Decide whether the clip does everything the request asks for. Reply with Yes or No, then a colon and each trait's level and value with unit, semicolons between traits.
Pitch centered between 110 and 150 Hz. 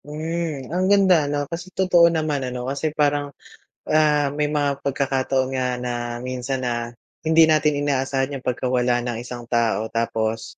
Yes: medium, 140 Hz